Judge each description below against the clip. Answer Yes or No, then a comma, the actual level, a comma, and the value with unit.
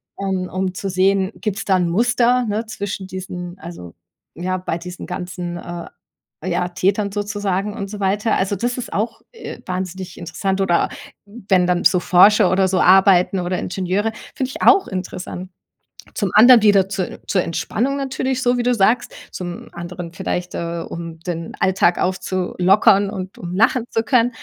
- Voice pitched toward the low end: No, high, 190 Hz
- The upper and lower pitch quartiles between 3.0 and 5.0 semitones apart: No, narrow, 2.6 semitones